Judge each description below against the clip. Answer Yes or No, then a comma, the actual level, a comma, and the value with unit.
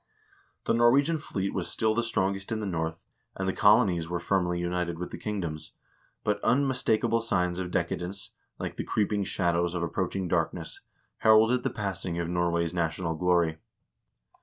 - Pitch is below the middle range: Yes, very low, 95 Hz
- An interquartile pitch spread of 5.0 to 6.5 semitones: No, average, 3.8 semitones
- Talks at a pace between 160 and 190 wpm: Yes, average, 165 wpm